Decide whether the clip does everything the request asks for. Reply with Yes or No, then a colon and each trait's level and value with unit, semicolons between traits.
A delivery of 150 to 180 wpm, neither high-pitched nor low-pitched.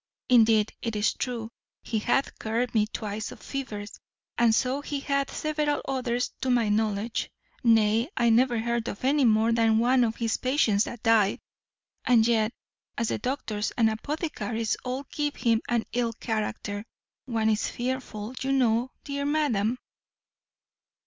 No: average, 155 wpm; high, 235 Hz